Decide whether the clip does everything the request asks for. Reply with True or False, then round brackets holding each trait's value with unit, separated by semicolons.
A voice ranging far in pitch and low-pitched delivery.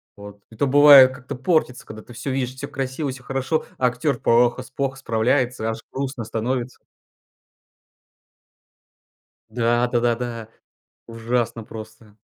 False (2.5 semitones; 125 Hz)